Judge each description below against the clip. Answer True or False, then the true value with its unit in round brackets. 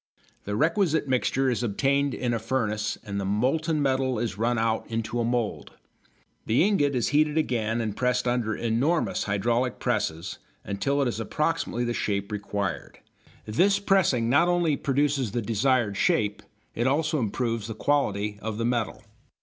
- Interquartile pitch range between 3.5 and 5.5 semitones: True (4.6 semitones)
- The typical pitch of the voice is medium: False (120 Hz)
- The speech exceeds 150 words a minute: True (160 wpm)